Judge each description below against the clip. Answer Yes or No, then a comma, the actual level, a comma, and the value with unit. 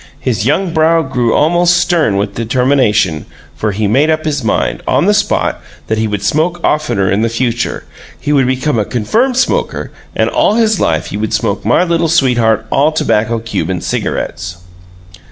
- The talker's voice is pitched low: Yes, low, 125 Hz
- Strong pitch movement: Yes, wide, 6.7 semitones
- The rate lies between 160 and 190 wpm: Yes, average, 175 wpm